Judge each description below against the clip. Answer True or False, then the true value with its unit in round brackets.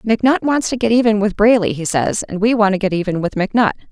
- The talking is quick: True (260 wpm)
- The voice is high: True (210 Hz)